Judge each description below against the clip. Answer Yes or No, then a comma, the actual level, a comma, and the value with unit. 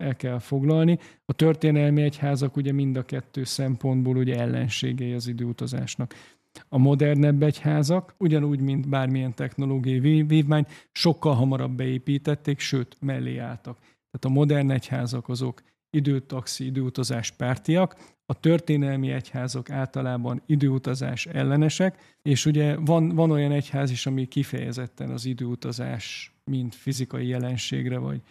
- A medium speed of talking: Yes, average, 125 wpm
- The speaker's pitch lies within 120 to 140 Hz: Yes, low, 135 Hz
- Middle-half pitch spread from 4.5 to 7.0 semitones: No, average, 2.7 semitones